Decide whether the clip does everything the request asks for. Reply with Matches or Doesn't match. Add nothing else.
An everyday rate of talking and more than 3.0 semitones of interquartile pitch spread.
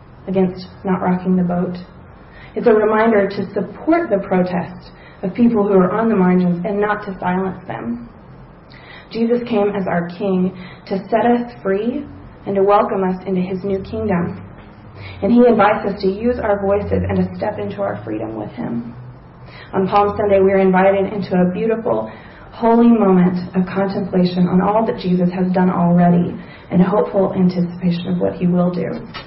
Doesn't match